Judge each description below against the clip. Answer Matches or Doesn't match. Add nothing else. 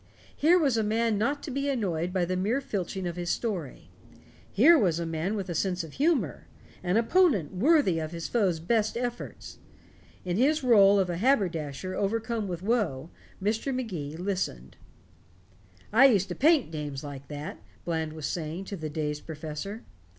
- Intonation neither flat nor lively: Doesn't match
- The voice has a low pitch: Doesn't match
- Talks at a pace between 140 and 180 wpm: Matches